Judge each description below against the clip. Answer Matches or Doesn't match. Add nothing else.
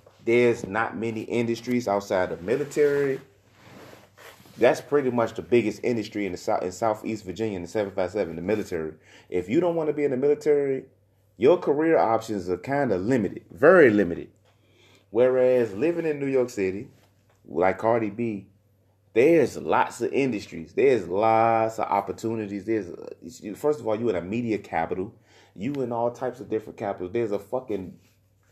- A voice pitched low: Matches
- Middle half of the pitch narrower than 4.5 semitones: Matches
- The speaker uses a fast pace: Doesn't match